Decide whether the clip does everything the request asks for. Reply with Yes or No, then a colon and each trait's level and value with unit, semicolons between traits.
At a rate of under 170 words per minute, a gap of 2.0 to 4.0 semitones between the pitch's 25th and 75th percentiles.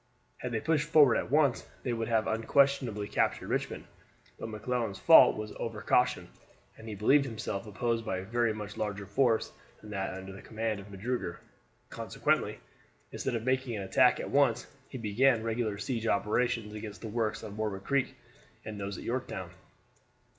No: average, 175 wpm; average, 3.0 semitones